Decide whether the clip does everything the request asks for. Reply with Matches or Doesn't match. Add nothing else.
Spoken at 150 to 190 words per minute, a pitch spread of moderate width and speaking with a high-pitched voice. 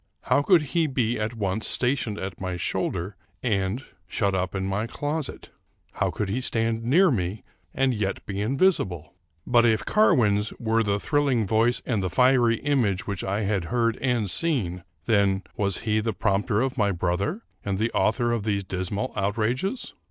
Doesn't match